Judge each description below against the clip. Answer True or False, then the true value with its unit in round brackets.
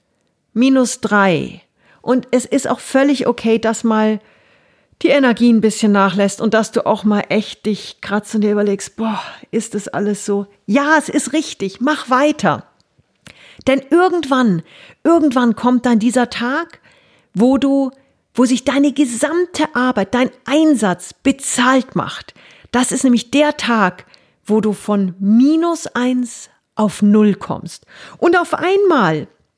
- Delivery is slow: False (140 wpm)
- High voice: True (240 Hz)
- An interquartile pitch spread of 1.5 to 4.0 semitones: False (4.7 semitones)